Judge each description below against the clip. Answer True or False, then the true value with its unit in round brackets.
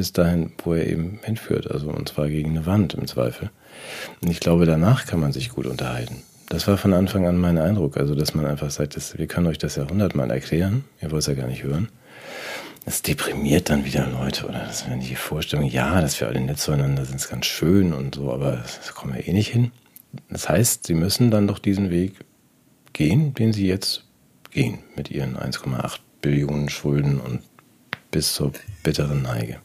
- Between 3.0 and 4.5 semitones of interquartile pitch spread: False (5.5 semitones)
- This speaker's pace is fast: True (205 wpm)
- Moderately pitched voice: False (80 Hz)